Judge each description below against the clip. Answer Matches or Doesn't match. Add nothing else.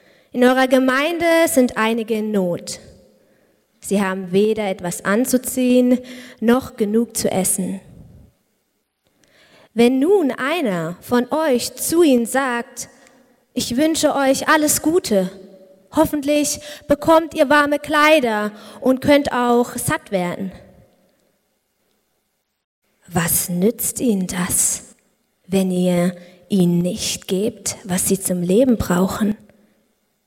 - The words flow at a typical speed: Doesn't match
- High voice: Matches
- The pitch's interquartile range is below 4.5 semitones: Doesn't match